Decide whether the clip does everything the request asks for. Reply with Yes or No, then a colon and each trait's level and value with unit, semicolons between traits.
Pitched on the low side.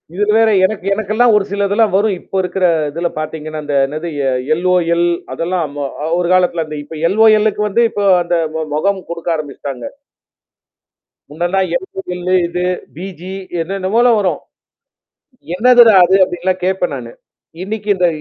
No: medium, 185 Hz